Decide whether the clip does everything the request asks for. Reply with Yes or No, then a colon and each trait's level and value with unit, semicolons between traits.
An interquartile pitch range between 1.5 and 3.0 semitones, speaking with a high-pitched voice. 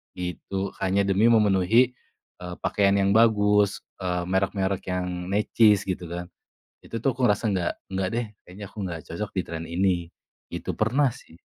No: average, 2.7 semitones; very low, 95 Hz